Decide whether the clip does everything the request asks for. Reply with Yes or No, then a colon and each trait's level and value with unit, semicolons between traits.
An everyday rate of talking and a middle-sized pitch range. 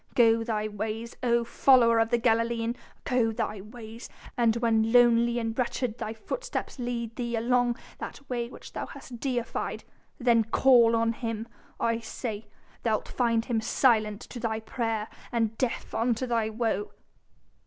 No: average, 155 wpm; narrow, 1.2 semitones